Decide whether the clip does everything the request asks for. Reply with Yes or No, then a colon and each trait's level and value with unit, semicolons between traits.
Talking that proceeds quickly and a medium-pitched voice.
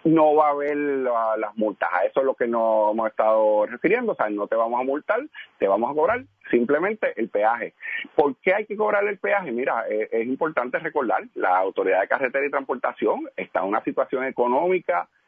Yes: fast, 205 wpm; medium, 145 Hz